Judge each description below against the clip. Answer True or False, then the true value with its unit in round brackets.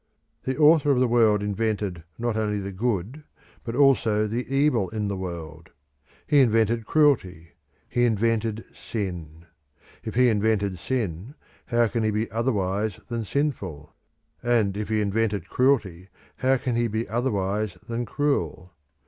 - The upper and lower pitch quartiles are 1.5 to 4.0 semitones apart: True (3.6 semitones)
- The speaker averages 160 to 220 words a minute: False (145 wpm)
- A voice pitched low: True (110 Hz)